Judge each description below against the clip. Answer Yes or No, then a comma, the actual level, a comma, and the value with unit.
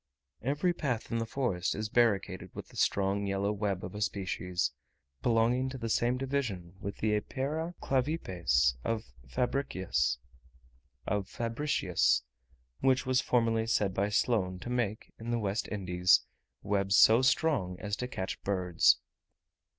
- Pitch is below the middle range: Yes, low, 105 Hz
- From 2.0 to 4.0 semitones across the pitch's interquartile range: No, average, 4.8 semitones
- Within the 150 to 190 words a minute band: No, slow, 135 wpm